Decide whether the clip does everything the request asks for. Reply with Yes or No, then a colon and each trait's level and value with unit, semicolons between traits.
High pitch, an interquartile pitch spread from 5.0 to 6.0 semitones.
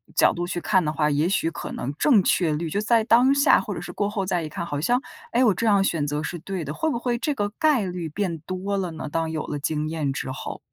No: medium, 180 Hz; wide, 5.4 semitones